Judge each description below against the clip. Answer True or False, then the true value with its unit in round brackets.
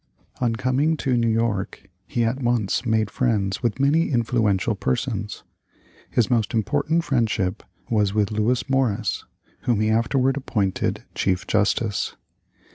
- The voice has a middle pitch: False (115 Hz)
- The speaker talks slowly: True (130 wpm)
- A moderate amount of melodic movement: True (3.3 semitones)